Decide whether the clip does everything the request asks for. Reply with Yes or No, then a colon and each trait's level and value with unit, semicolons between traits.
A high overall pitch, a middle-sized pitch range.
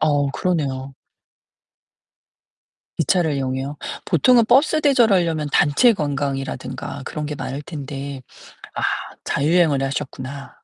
No: medium, 145 Hz; average, 4.1 semitones